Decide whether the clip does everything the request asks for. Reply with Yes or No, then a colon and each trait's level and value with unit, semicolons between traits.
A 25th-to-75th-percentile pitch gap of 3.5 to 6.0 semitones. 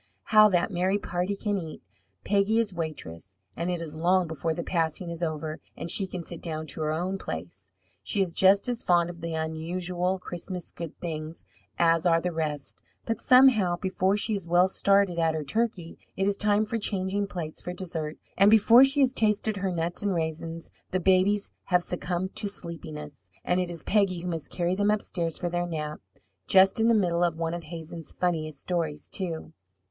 No: average, 3.1 semitones